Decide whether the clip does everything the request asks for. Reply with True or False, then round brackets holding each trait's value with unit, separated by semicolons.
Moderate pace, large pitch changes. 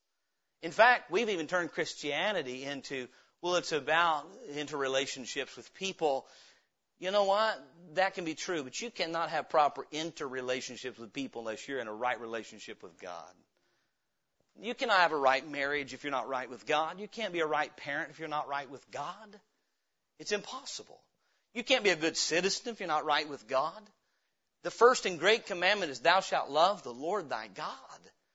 True (185 wpm; 6.1 semitones)